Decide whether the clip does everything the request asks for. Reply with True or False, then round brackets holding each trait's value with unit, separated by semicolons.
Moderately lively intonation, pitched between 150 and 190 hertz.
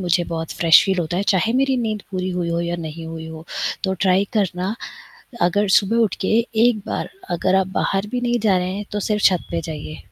True (3.5 semitones; 185 Hz)